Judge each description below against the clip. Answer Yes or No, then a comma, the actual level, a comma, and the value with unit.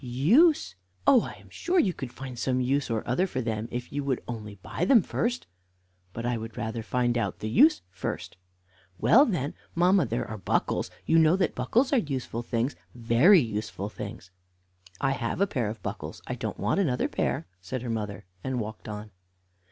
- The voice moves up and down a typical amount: No, wide, 6.4 semitones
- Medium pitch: No, low, 125 Hz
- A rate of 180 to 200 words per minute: Yes, average, 190 wpm